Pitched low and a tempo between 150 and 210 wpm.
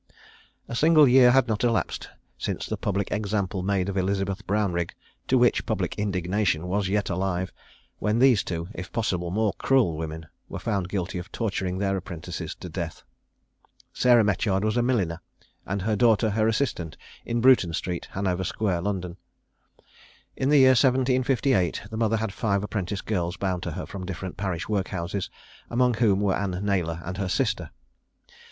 Yes: low, 100 Hz; average, 170 wpm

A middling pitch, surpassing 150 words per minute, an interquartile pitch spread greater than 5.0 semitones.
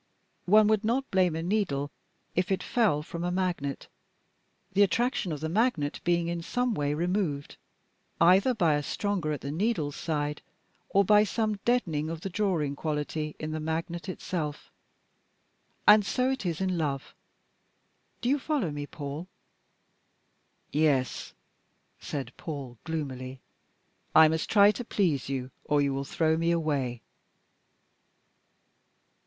No: medium, 165 Hz; average, 140 wpm; wide, 5.4 semitones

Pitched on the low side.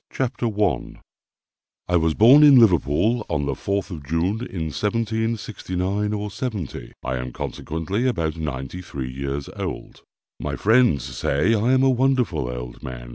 Yes: very low, 95 Hz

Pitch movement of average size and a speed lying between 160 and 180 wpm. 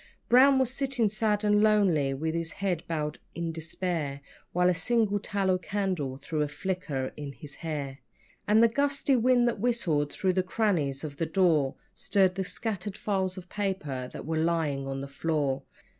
No: wide, 5.7 semitones; average, 175 wpm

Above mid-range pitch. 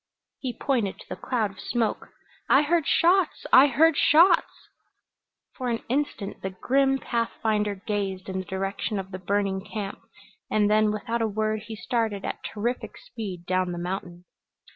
Yes: high, 215 Hz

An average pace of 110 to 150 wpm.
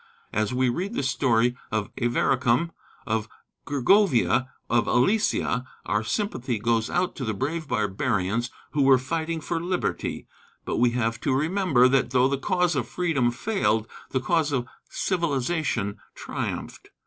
Yes: average, 145 wpm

